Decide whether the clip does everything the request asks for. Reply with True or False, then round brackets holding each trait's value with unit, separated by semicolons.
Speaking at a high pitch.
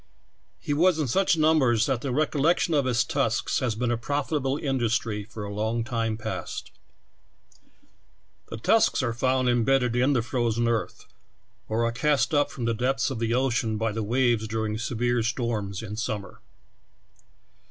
False (120 Hz)